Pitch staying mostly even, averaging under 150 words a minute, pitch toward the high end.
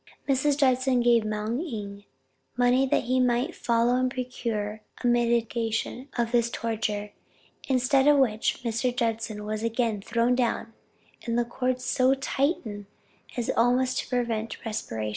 Yes: narrow, 2.3 semitones; average, 140 wpm; high, 240 Hz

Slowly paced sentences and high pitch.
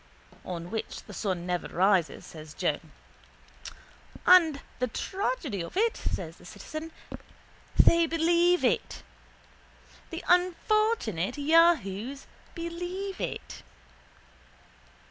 Yes: slow, 100 wpm; very high, 310 Hz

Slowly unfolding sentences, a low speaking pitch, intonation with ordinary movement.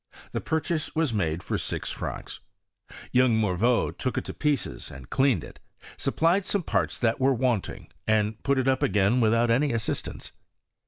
No: average, 175 wpm; low, 125 Hz; average, 4.3 semitones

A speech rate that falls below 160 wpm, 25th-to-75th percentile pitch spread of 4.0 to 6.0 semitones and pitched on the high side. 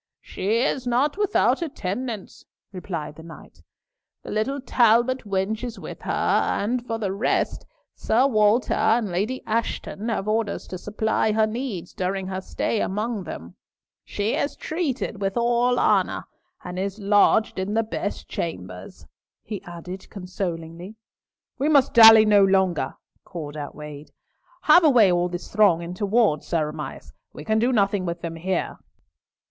Yes: average, 150 wpm; average, 4.4 semitones; high, 205 Hz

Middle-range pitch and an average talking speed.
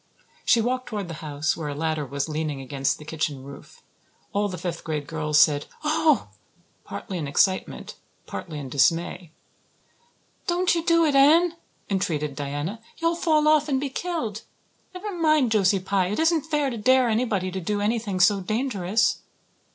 No: high, 200 Hz; average, 165 wpm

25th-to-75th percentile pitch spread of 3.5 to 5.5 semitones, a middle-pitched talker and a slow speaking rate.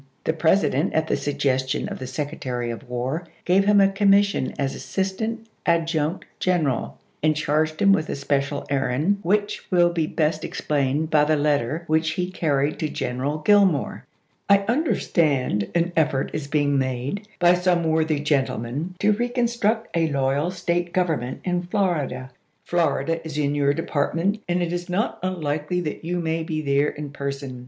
No: average, 4.0 semitones; medium, 160 Hz; average, 170 wpm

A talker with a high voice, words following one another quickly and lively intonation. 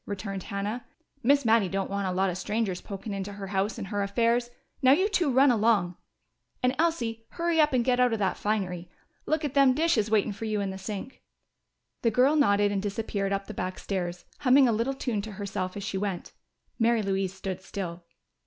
No: high, 210 Hz; fast, 210 wpm; average, 4.1 semitones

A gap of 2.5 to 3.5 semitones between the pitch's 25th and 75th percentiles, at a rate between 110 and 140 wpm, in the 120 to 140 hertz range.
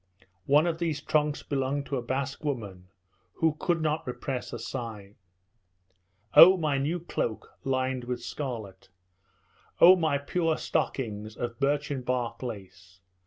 No: average, 4.2 semitones; slow, 135 wpm; low, 135 Hz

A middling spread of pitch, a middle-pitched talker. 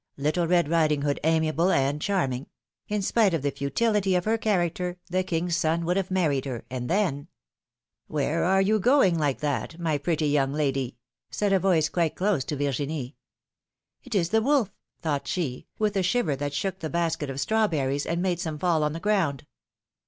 Yes: average, 4.7 semitones; medium, 165 Hz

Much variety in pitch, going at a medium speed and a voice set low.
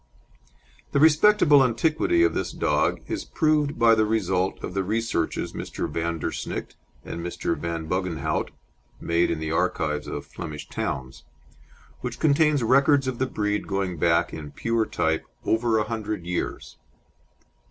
Yes: wide, 8.3 semitones; average, 150 wpm; low, 105 Hz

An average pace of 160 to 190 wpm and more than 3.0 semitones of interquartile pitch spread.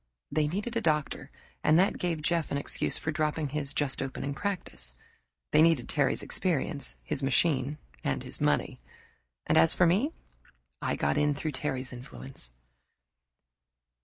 No: average, 150 wpm; average, 3.5 semitones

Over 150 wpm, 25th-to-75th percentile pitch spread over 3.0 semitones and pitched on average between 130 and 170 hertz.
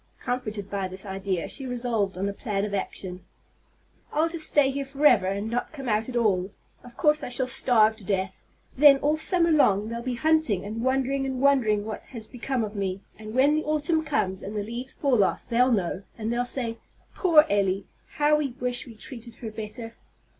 No: fast, 205 wpm; average, 4.9 semitones; high, 235 Hz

